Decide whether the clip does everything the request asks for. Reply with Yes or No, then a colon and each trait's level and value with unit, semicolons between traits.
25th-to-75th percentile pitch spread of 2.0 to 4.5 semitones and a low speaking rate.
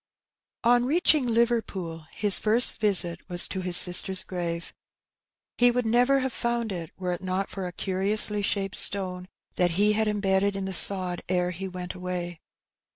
No: average, 3.4 semitones; average, 165 wpm